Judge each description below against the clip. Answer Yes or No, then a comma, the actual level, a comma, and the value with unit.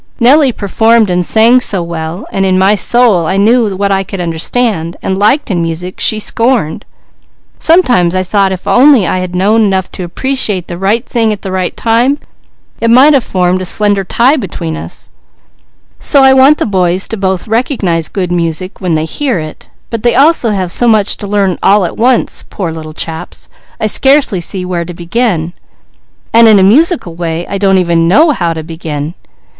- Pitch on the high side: Yes, high, 195 Hz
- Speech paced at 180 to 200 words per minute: Yes, average, 190 wpm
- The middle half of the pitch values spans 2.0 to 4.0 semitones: No, average, 4.8 semitones